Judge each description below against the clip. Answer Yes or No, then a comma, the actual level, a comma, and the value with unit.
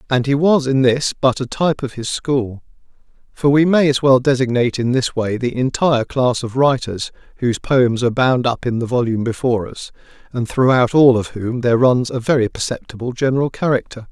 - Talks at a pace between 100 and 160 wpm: No, average, 200 wpm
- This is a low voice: Yes, low, 125 Hz